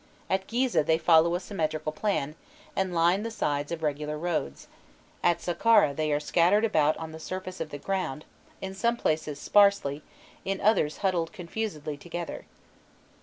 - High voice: No, medium, 170 Hz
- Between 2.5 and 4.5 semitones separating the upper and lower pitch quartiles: Yes, average, 4.0 semitones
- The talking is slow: No, average, 160 wpm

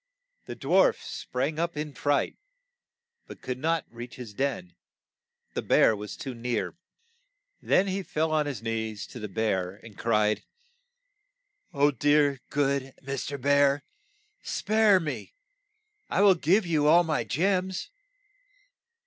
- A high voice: No, medium, 140 Hz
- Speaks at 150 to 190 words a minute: No, slow, 135 wpm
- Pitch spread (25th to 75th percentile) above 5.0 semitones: Yes, wide, 5.5 semitones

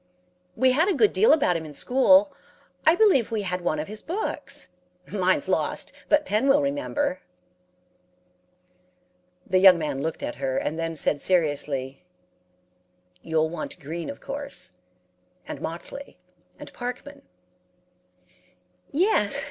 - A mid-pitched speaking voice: No, high, 205 Hz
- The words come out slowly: Yes, slow, 130 wpm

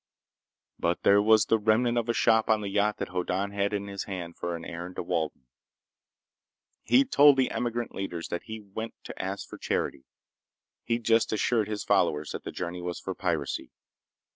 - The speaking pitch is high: No, low, 100 Hz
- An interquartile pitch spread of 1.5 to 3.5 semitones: No, average, 4.1 semitones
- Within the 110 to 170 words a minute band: No, average, 185 wpm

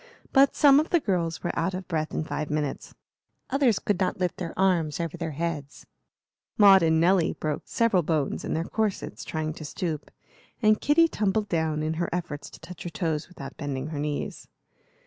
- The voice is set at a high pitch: No, medium, 170 Hz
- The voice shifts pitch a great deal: No, average, 3.8 semitones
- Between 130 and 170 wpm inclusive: No, average, 190 wpm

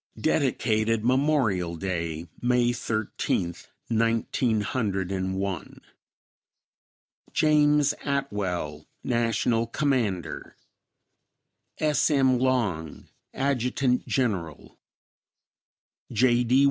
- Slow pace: Yes, slow, 70 wpm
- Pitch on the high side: No, low, 115 Hz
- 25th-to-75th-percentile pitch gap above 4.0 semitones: Yes, wide, 5.4 semitones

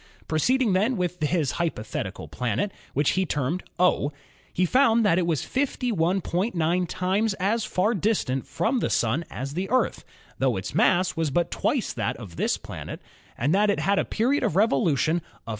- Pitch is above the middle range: No, medium, 180 Hz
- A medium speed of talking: Yes, average, 175 wpm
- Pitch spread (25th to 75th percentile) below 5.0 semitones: No, wide, 5.5 semitones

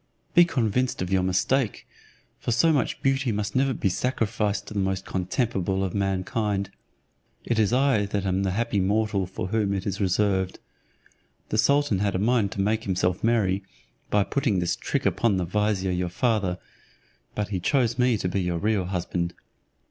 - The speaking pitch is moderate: No, low, 100 Hz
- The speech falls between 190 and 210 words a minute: No, average, 180 wpm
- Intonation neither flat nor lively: Yes, average, 3.4 semitones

